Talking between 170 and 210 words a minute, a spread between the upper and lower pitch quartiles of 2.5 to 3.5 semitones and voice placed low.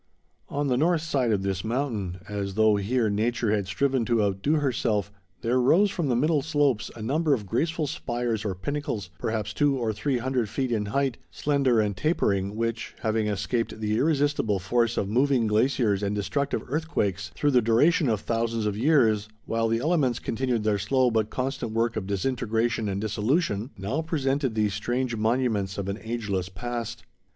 No: average, 175 wpm; average, 4.4 semitones; low, 115 Hz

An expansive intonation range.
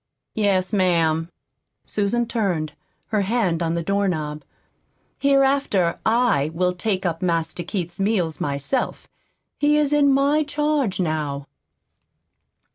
Yes: wide, 6.5 semitones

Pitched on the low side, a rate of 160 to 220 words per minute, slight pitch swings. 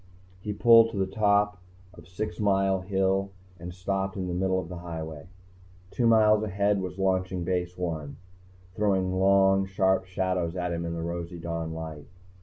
Yes: very low, 95 Hz; average, 170 wpm; narrow, 2.0 semitones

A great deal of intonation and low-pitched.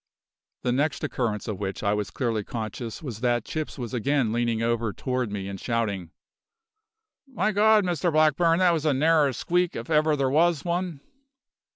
Yes: wide, 6.1 semitones; low, 130 Hz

